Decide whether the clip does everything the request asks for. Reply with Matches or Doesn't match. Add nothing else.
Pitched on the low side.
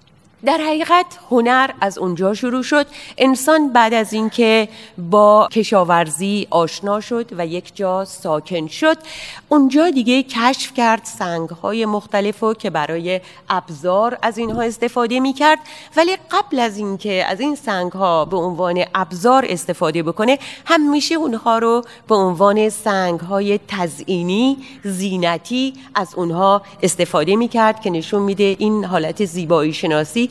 Doesn't match